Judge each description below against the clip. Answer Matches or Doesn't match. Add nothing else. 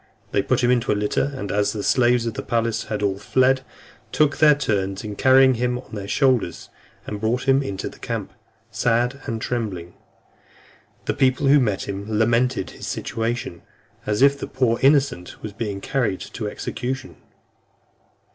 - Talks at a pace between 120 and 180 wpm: Matches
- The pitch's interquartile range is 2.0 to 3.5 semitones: Doesn't match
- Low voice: Matches